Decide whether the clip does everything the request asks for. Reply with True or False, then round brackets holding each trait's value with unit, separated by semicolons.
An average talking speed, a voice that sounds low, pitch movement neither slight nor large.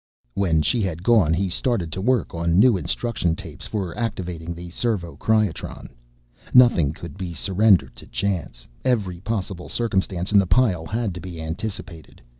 True (160 wpm; 95 Hz; 4.3 semitones)